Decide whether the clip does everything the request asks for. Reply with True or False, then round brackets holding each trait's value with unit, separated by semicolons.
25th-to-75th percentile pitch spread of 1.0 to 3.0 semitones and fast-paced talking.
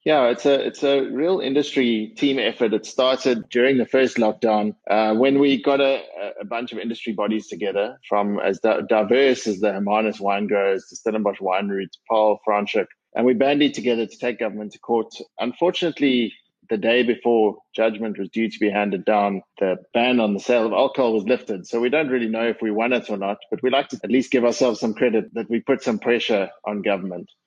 False (3.4 semitones; 215 wpm)